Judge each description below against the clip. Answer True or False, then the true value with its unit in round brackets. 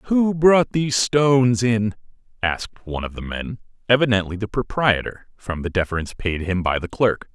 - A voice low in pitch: True (110 Hz)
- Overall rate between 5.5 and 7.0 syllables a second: False (5.1 syllables/s)